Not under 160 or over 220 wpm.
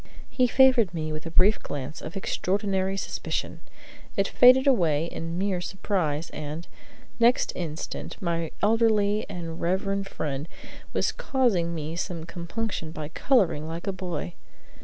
No: average, 140 wpm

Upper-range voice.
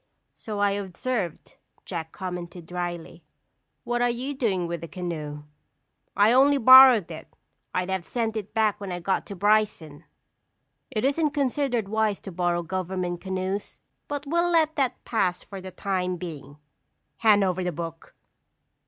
Yes: high, 195 Hz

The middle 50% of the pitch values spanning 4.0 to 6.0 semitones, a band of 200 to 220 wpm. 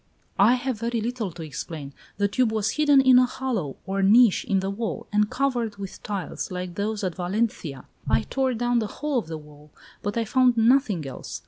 Yes: average, 5.1 semitones; fast, 205 wpm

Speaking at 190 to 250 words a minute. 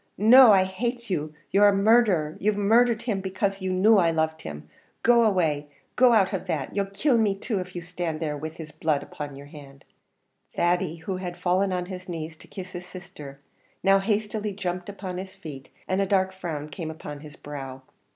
Yes: average, 200 wpm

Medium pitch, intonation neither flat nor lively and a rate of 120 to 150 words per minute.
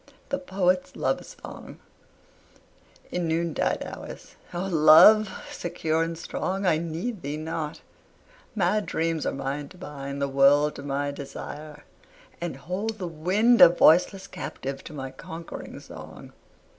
Yes: medium, 165 Hz; average, 3.8 semitones; average, 140 wpm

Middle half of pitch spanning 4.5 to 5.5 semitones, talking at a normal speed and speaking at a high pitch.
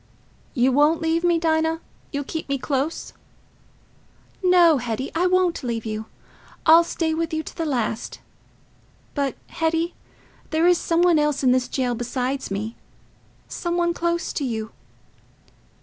Yes: average, 4.8 semitones; average, 150 wpm; very high, 315 Hz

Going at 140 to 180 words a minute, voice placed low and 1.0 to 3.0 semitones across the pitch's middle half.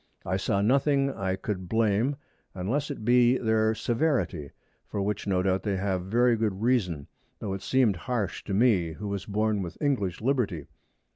No: average, 170 wpm; low, 105 Hz; average, 4.3 semitones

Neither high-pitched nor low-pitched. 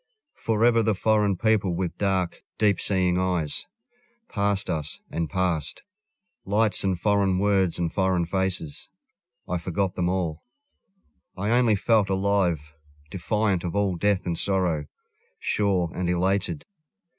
No: very low, 95 Hz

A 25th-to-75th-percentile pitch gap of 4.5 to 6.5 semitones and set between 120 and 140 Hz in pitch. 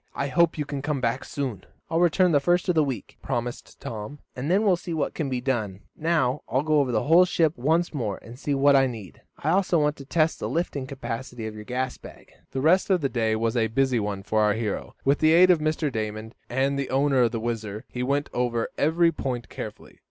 Yes: average, 4.9 semitones; low, 135 Hz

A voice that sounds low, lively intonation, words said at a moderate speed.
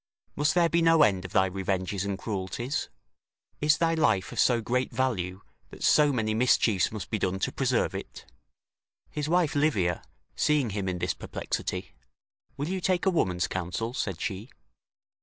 Yes: low, 110 Hz; wide, 8.0 semitones; average, 170 wpm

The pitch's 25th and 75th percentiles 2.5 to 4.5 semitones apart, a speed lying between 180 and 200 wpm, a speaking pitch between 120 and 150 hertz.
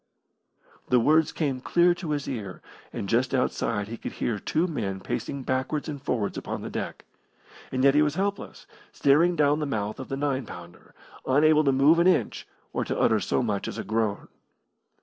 No: average, 5.1 semitones; average, 190 wpm; low, 135 Hz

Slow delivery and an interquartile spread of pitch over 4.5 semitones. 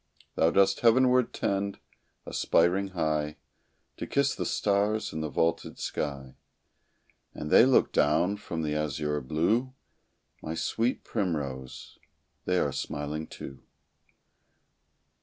Yes: slow, 120 wpm; wide, 5.4 semitones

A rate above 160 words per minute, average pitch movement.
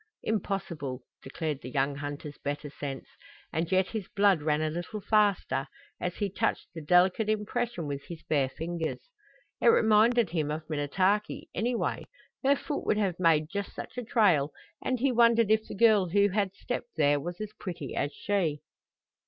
No: average, 170 wpm; wide, 5.9 semitones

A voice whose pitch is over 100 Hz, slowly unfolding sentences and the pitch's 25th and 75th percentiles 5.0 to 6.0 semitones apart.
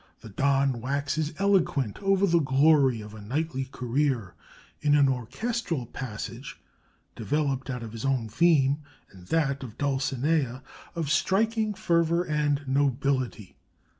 No: medium, 140 Hz; slow, 130 wpm; average, 3.8 semitones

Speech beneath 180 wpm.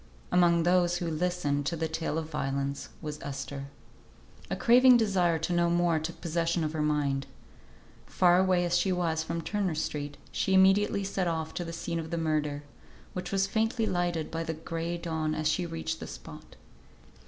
No: average, 185 wpm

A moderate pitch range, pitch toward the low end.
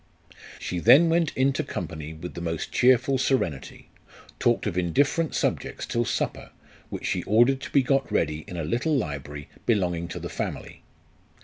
No: wide, 8.3 semitones; low, 105 Hz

